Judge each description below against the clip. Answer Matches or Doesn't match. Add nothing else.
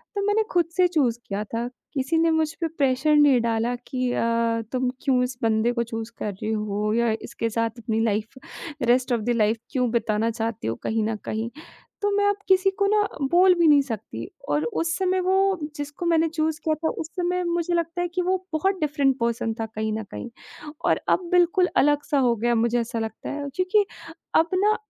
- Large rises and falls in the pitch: Matches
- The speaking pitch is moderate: Doesn't match